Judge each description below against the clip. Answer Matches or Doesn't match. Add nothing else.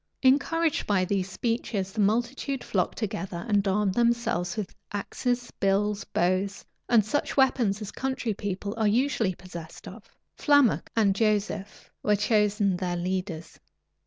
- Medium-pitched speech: Doesn't match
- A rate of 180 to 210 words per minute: Doesn't match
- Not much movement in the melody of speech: Doesn't match